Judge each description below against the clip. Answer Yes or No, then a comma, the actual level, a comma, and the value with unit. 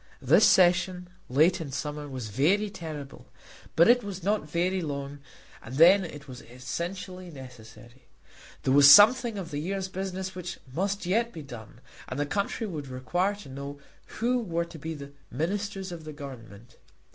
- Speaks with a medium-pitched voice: Yes, medium, 165 Hz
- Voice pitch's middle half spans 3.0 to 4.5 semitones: No, wide, 5.5 semitones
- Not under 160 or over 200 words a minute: Yes, average, 170 wpm